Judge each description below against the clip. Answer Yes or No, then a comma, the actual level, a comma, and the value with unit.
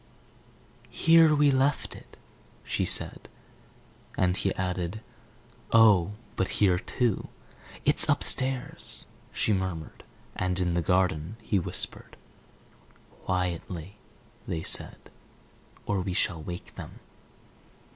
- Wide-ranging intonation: No, average, 3.7 semitones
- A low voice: Yes, very low, 95 Hz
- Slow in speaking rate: Yes, slow, 105 wpm